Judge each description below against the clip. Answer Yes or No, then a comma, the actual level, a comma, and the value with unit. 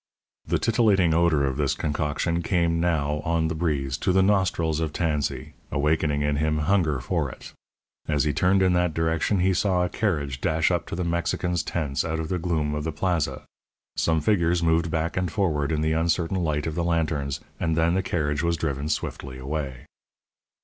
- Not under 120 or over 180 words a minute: No, average, 190 wpm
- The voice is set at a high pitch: No, very low, 80 Hz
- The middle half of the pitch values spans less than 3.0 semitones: Yes, narrow, 2.6 semitones